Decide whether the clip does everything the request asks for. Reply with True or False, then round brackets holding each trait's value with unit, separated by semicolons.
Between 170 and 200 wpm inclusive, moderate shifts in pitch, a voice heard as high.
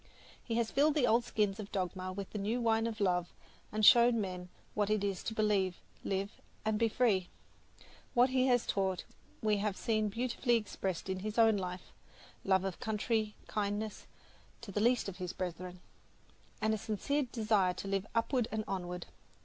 True (180 wpm; 3.1 semitones; 210 Hz)